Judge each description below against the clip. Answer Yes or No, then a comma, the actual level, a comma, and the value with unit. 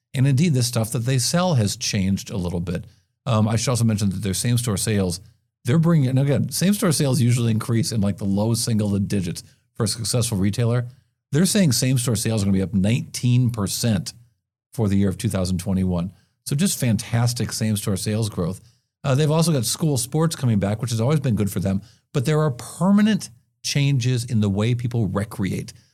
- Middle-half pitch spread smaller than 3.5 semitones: No, average, 4.1 semitones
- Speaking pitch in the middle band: No, low, 115 Hz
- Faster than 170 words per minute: Yes, fast, 205 wpm